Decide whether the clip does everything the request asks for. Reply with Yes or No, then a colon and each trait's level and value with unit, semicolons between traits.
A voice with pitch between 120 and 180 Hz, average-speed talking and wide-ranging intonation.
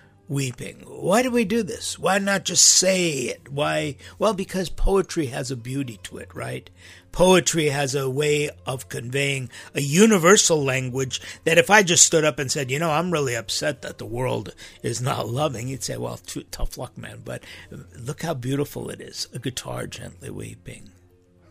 Yes: medium, 140 Hz; average, 185 wpm; wide, 5.8 semitones